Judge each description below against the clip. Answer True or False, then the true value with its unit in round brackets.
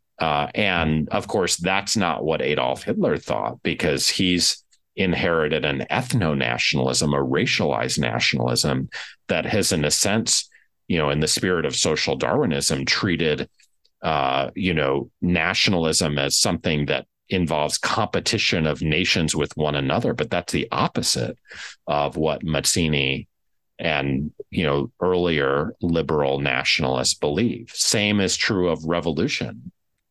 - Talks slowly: True (130 wpm)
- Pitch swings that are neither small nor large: True (3.3 semitones)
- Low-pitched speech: True (75 Hz)